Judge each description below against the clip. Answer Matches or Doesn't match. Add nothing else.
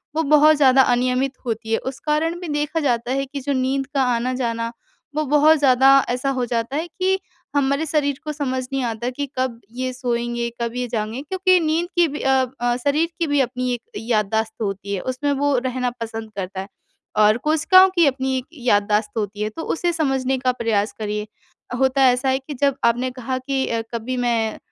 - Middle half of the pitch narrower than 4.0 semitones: Matches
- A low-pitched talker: Doesn't match